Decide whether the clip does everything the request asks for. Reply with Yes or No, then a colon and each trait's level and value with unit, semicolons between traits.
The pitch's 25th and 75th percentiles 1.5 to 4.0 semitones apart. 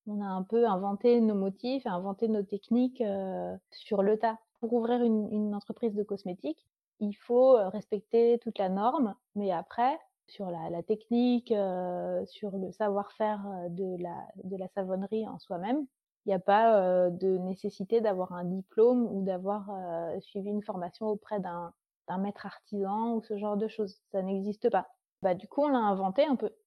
Yes: average, 3.1 semitones